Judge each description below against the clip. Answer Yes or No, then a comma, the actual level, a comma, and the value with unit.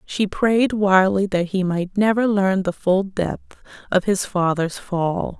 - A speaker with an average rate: Yes, average, 165 wpm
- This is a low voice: No, high, 190 Hz